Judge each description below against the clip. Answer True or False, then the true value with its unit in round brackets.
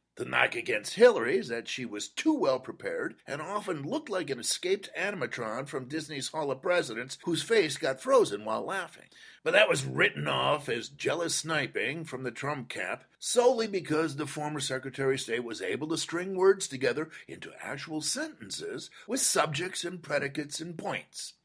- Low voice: False (165 Hz)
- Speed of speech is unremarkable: True (175 wpm)